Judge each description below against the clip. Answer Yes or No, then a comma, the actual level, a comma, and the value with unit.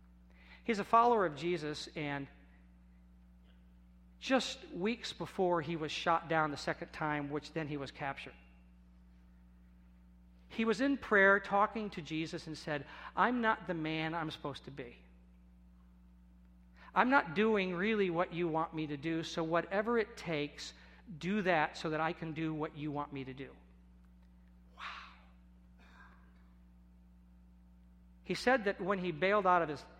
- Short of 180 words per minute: Yes, average, 150 wpm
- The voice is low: No, medium, 150 Hz